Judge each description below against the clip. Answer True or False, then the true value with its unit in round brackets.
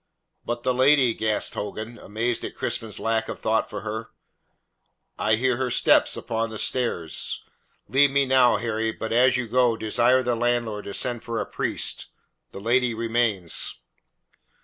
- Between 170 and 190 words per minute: False (160 wpm)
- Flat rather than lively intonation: True (2.1 semitones)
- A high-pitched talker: False (115 Hz)